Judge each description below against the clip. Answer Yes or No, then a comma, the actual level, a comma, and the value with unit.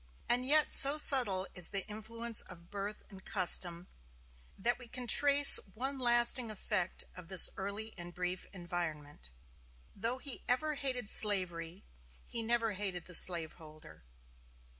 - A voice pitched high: Yes, high, 205 Hz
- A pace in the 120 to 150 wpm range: Yes, average, 140 wpm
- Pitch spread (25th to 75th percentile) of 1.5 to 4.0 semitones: No, average, 5.2 semitones